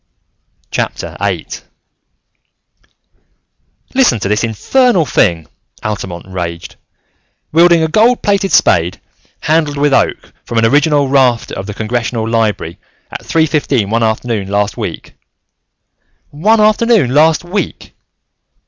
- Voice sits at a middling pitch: No, low, 130 Hz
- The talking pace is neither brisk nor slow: No, slow, 115 wpm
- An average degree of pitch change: No, wide, 7.4 semitones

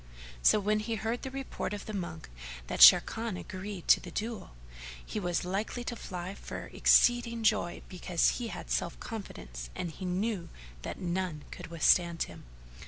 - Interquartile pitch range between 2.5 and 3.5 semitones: No, average, 4.3 semitones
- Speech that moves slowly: No, average, 170 wpm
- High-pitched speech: Yes, high, 195 Hz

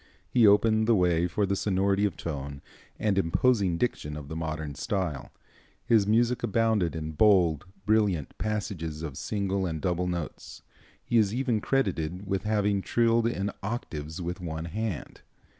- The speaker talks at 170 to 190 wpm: No, average, 155 wpm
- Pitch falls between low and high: No, very low, 95 Hz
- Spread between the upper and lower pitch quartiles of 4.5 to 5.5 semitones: Yes, average, 4.9 semitones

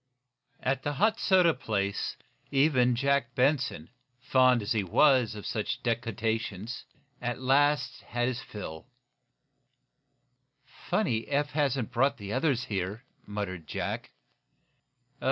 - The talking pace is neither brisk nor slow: No, slow, 115 wpm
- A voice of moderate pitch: No, low, 125 Hz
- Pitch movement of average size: Yes, average, 4.3 semitones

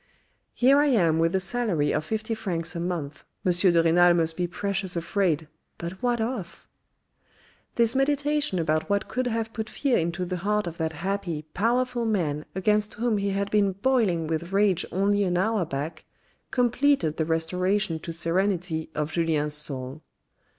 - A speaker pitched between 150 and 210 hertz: Yes, medium, 185 Hz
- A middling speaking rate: Yes, average, 170 wpm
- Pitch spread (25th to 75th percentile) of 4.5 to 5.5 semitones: Yes, average, 4.9 semitones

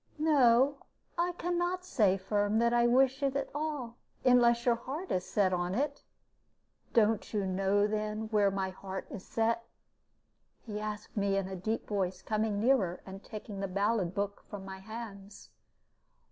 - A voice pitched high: Yes, high, 215 Hz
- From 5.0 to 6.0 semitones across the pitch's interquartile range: No, average, 3.9 semitones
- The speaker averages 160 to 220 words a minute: Yes, average, 170 wpm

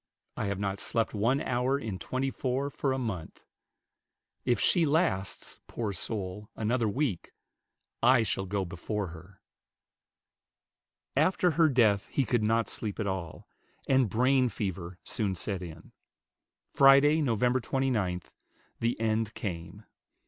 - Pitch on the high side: No, low, 110 Hz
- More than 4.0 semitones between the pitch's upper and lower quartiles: Yes, average, 5.2 semitones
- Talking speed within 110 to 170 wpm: Yes, slow, 135 wpm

